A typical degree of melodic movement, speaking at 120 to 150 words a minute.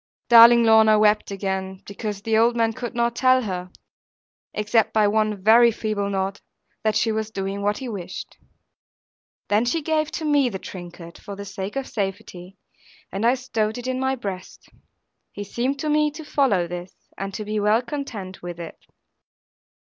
No: average, 3.6 semitones; average, 175 wpm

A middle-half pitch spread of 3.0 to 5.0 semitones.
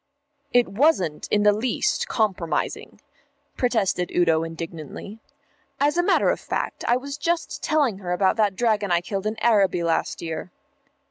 No: wide, 5.5 semitones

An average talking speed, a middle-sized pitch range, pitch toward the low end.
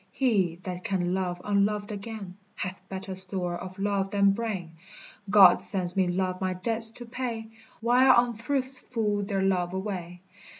No: average, 155 wpm; average, 3.3 semitones; high, 195 Hz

